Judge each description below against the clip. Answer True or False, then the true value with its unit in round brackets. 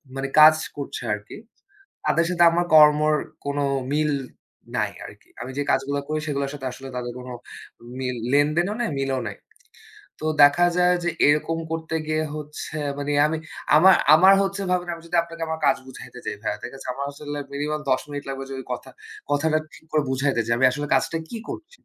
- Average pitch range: True (3.1 semitones)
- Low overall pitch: False (150 Hz)